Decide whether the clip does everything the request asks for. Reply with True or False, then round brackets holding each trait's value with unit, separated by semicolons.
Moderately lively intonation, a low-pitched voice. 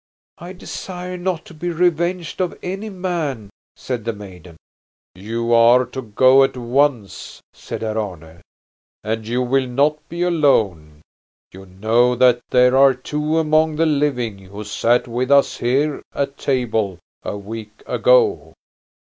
False (5.9 semitones; 125 Hz)